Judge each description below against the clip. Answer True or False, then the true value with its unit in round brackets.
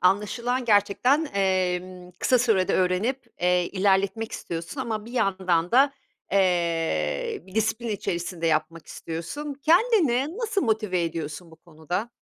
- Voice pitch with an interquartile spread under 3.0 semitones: False (5.6 semitones)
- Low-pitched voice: False (195 Hz)